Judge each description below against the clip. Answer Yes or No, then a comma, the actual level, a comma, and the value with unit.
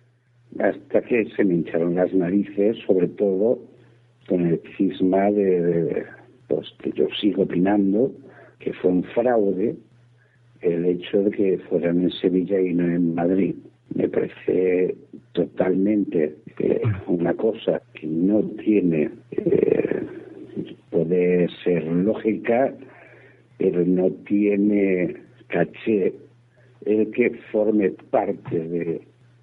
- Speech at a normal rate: No, slow, 115 wpm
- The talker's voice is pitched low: Yes, very low, 95 Hz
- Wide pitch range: No, average, 4.5 semitones